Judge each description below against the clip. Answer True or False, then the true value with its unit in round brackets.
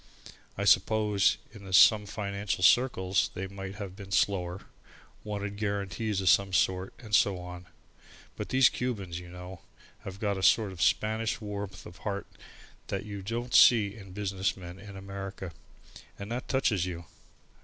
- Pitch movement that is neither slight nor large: False (2.1 semitones)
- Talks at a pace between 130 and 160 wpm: True (155 wpm)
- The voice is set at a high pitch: False (100 Hz)